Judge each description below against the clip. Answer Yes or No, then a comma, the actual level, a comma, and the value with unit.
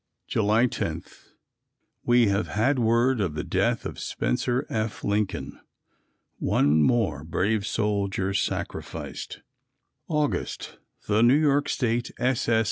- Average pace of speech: No, slow, 120 wpm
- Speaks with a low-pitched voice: Yes, low, 110 Hz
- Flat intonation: No, average, 3.6 semitones